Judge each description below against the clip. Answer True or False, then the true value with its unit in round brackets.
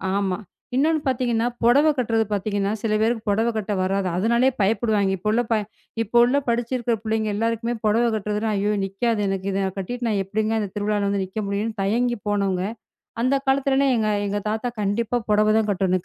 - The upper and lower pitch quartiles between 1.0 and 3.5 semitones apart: True (2.8 semitones)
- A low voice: False (215 Hz)